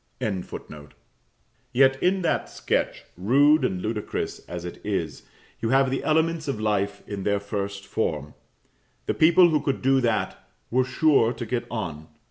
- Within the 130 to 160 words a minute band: Yes, average, 155 wpm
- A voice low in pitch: Yes, low, 115 Hz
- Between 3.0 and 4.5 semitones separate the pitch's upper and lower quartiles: No, wide, 5.5 semitones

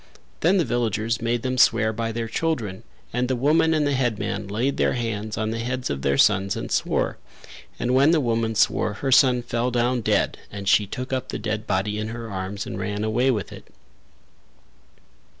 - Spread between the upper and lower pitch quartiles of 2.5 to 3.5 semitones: Yes, average, 3.2 semitones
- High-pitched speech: No, low, 115 Hz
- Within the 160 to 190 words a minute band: No, average, 200 wpm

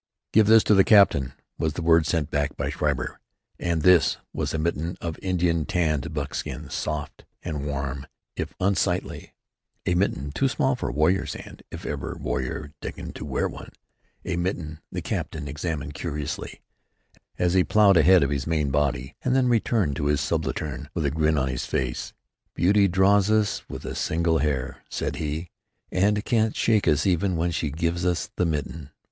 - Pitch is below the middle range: Yes, very low, 80 Hz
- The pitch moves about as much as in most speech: Yes, average, 4.3 semitones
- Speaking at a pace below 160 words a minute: No, average, 180 wpm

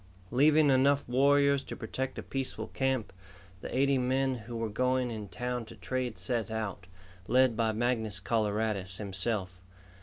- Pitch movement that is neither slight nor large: Yes, average, 3.4 semitones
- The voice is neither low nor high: No, low, 120 Hz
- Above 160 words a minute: No, average, 150 wpm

